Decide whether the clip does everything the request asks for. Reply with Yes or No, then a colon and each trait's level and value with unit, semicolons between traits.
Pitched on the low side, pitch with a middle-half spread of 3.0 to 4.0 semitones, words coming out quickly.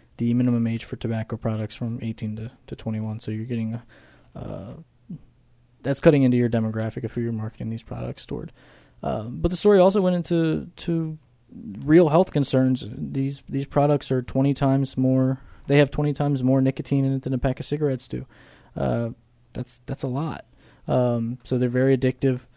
No: low, 130 Hz; average, 3.3 semitones; average, 185 wpm